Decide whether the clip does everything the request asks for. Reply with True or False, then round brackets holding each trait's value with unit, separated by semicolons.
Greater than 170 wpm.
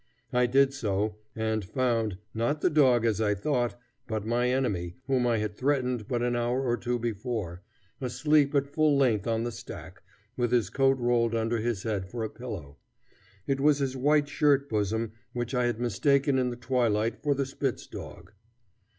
True (185 wpm)